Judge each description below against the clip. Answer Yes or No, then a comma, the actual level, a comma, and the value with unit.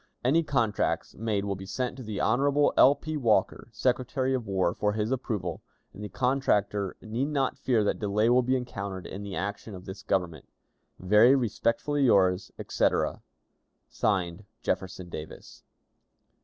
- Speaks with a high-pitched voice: No, low, 105 Hz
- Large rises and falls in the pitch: No, average, 4.7 semitones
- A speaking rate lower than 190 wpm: Yes, average, 155 wpm